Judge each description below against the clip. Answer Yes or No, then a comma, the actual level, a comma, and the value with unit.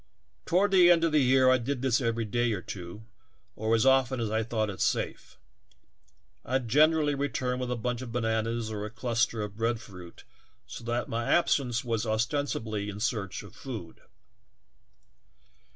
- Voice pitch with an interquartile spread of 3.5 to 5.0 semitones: No, average, 3.1 semitones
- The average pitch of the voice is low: Yes, low, 120 Hz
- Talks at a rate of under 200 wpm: Yes, average, 170 wpm